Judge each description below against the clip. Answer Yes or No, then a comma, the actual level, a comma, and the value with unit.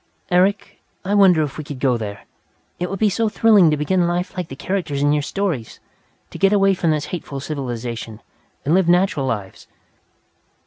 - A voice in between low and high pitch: Yes, medium, 165 Hz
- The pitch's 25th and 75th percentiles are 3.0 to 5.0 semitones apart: No, wide, 5.5 semitones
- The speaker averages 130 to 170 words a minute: No, average, 185 wpm